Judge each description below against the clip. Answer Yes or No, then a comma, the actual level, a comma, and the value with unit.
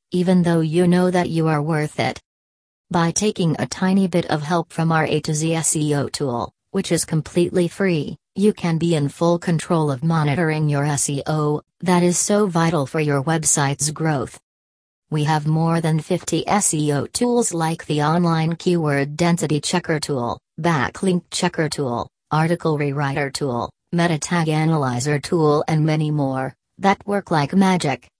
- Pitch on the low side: No, medium, 160 Hz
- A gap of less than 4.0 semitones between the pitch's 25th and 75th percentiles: Yes, average, 2.8 semitones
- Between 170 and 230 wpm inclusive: No, average, 160 wpm